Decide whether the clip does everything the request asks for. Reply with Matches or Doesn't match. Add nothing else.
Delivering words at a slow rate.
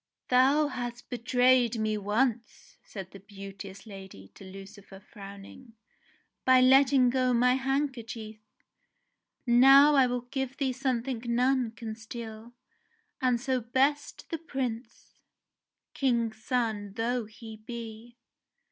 Matches